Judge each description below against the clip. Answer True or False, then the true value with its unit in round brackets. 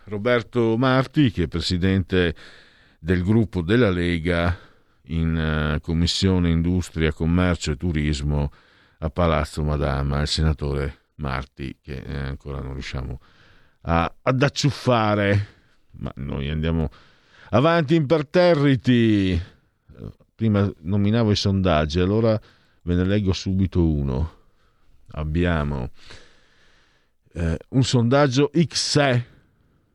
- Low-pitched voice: True (90 Hz)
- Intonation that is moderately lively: False (6.4 semitones)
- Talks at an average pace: False (100 wpm)